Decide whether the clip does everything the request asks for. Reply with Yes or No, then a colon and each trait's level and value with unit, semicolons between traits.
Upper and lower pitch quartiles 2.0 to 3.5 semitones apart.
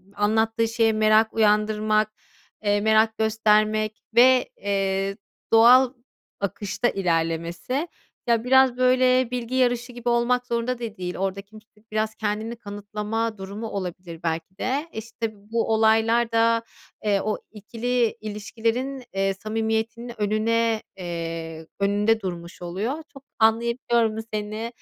Yes: narrow, 2.4 semitones